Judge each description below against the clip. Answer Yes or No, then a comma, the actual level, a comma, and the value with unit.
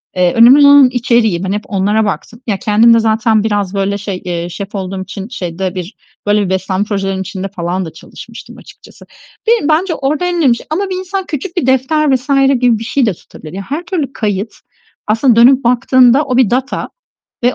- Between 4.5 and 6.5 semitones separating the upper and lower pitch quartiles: Yes, wide, 5.6 semitones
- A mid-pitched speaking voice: No, high, 225 Hz